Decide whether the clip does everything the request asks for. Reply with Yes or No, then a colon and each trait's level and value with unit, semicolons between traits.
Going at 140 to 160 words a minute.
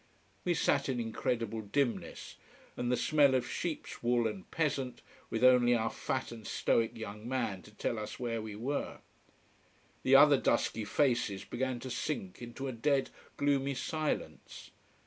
Yes: average, 155 wpm